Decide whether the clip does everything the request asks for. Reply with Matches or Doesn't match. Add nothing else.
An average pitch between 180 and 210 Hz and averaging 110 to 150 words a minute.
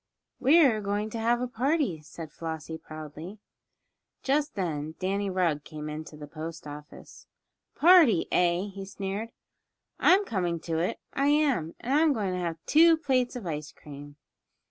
Doesn't match